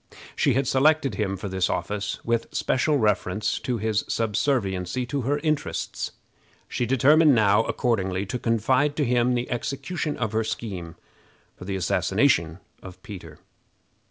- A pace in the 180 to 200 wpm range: No, average, 145 wpm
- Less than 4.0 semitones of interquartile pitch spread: No, average, 5.3 semitones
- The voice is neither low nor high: No, low, 115 Hz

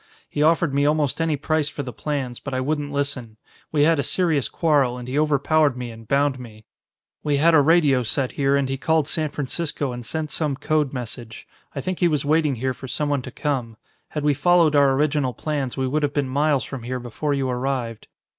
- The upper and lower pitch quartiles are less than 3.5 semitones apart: Yes, average, 2.8 semitones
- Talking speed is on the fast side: Yes, fast, 220 wpm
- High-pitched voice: No, medium, 140 Hz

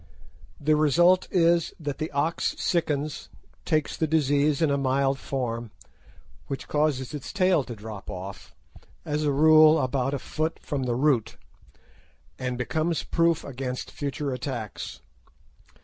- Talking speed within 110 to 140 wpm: Yes, slow, 135 wpm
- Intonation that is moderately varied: Yes, average, 3.2 semitones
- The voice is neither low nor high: Yes, medium, 145 Hz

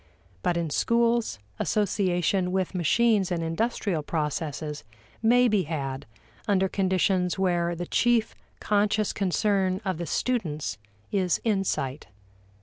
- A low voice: No, medium, 185 Hz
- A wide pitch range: No, average, 3.9 semitones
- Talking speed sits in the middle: No, slow, 115 wpm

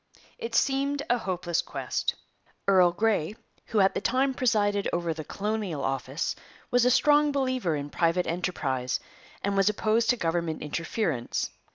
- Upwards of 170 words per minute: No, average, 150 wpm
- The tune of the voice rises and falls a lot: Yes, wide, 6.6 semitones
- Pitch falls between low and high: No, high, 195 Hz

